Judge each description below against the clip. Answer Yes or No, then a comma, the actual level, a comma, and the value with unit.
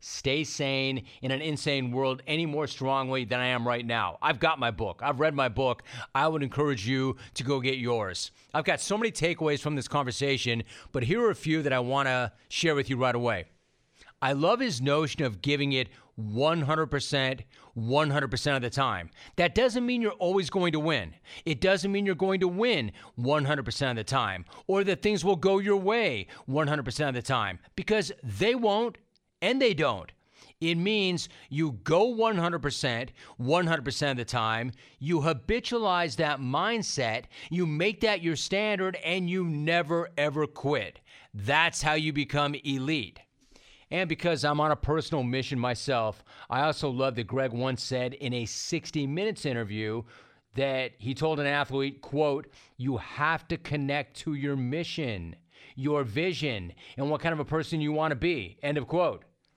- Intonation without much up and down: No, average, 4.3 semitones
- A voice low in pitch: No, medium, 145 Hz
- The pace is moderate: Yes, average, 175 wpm